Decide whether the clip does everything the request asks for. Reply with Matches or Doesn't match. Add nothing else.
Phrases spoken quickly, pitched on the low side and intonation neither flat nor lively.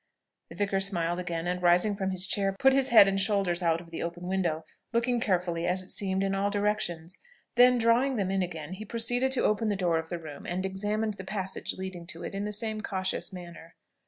Doesn't match